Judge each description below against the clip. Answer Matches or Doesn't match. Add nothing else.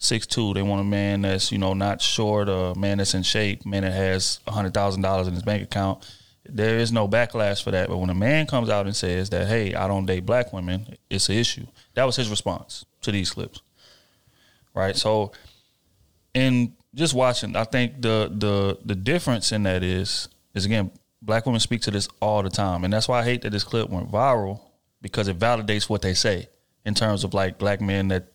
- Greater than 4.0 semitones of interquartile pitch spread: Doesn't match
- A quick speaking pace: Matches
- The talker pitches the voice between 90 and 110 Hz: Matches